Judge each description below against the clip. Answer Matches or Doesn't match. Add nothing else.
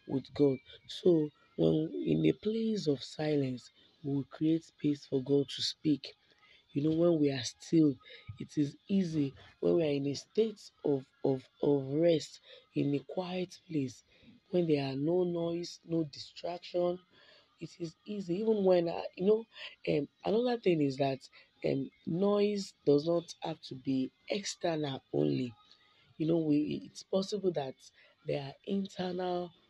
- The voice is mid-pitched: Matches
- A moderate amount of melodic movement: Matches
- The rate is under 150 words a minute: Doesn't match